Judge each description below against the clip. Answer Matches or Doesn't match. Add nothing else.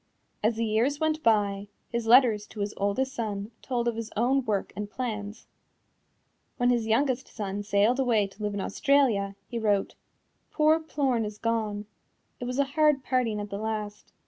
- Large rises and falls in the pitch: Doesn't match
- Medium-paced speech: Matches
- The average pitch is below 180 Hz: Doesn't match